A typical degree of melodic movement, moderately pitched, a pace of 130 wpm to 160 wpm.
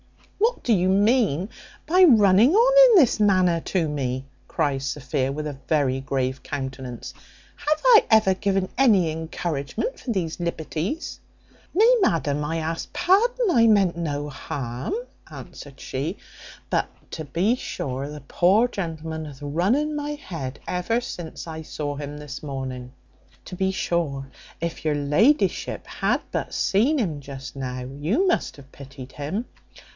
No: wide, 7.6 semitones; medium, 165 Hz; average, 150 wpm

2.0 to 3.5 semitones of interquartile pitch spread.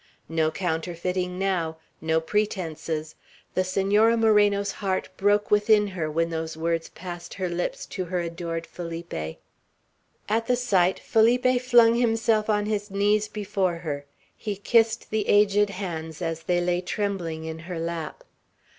No: average, 3.9 semitones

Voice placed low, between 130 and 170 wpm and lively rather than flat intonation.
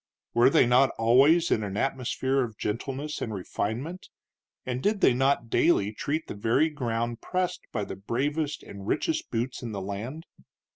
No: low, 125 Hz; average, 165 wpm; average, 4.5 semitones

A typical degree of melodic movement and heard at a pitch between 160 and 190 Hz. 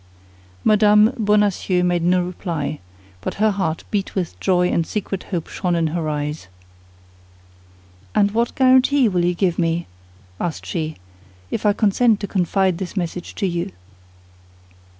Yes: average, 3.4 semitones; medium, 185 Hz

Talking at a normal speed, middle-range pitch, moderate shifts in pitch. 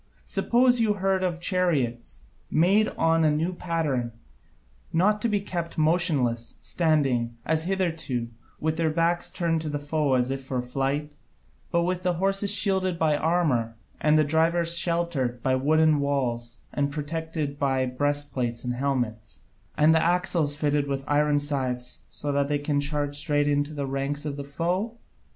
Yes: average, 160 wpm; medium, 150 Hz; average, 3.7 semitones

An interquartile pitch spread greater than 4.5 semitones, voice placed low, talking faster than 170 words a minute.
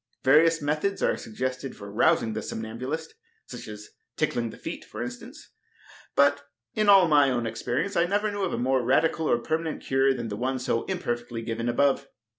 Yes: average, 5.1 semitones; low, 130 Hz; average, 185 wpm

